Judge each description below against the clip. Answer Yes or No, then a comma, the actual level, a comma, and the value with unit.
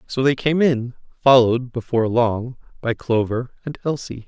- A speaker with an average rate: Yes, average, 155 wpm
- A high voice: No, low, 125 Hz